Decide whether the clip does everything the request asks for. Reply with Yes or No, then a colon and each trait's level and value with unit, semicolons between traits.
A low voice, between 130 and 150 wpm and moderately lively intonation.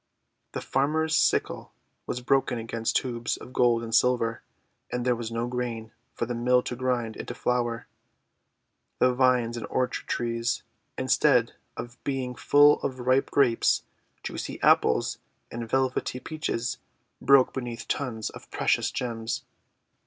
No: low, 125 Hz; average, 140 wpm; narrow, 1.8 semitones